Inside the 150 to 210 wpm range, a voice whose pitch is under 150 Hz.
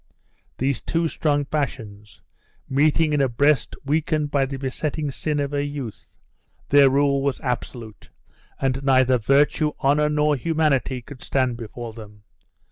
No: average, 140 wpm; medium, 140 Hz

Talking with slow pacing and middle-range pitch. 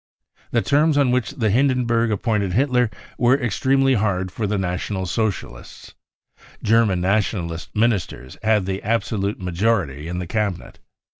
No: slow, 130 wpm; low, 105 Hz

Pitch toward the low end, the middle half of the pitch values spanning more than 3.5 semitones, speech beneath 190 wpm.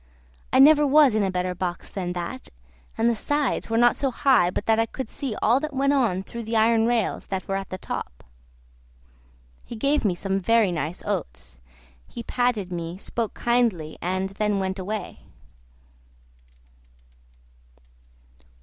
No: high, 215 Hz; average, 4.7 semitones; average, 160 wpm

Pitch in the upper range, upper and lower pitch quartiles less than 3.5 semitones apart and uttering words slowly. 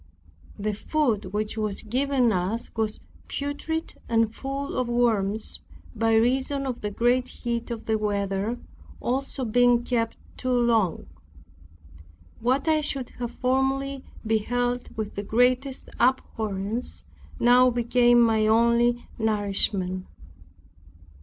Yes: high, 235 Hz; average, 2.9 semitones; slow, 115 wpm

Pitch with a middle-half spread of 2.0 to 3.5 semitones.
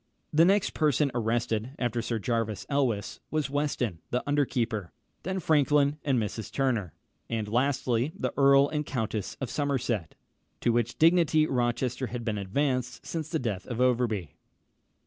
No: average, 4.0 semitones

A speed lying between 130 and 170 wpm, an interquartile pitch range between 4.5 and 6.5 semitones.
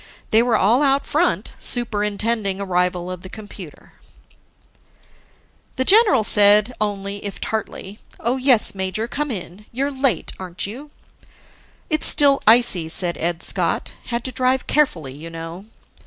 Yes: average, 140 wpm; average, 5.3 semitones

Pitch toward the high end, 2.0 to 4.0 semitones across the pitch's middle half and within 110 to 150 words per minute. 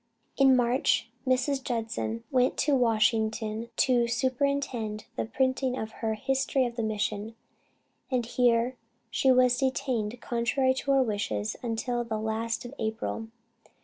Yes: high, 240 Hz; average, 2.8 semitones; slow, 135 wpm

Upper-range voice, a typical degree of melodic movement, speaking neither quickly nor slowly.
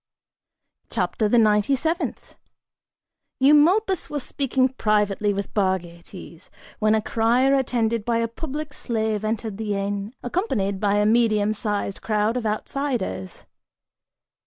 No: high, 220 Hz; average, 3.8 semitones; slow, 120 wpm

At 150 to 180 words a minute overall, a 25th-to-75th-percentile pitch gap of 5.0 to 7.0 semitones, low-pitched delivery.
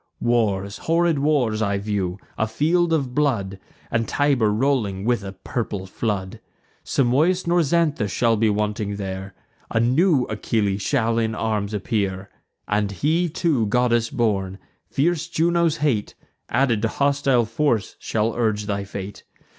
No: average, 140 wpm; wide, 5.6 semitones; low, 115 Hz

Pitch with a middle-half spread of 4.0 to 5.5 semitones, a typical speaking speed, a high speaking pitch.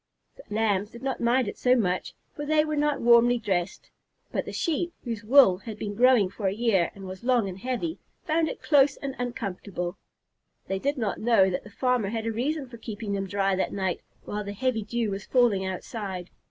No: average, 4.5 semitones; fast, 215 wpm; high, 225 Hz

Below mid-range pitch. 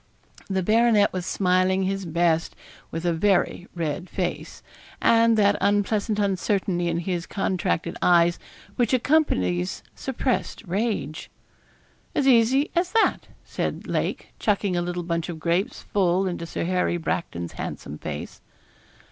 No: medium, 185 Hz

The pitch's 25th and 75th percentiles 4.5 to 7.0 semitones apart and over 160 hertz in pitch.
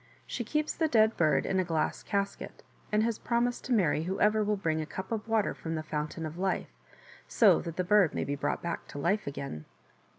Yes: wide, 5.5 semitones; high, 190 Hz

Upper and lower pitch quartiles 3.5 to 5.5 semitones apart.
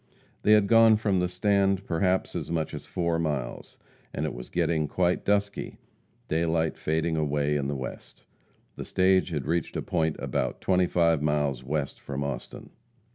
Yes: average, 4.0 semitones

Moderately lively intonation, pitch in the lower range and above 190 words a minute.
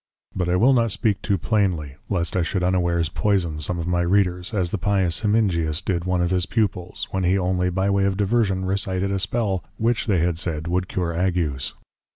No: narrow, 2.2 semitones; very low, 90 Hz; fast, 205 wpm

